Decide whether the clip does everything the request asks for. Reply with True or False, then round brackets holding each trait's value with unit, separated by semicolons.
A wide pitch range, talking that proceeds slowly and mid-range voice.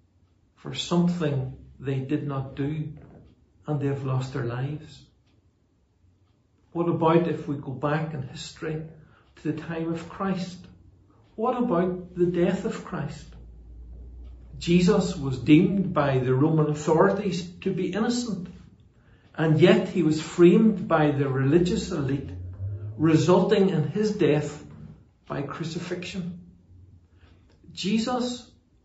True (7.4 semitones; 120 wpm; 150 Hz)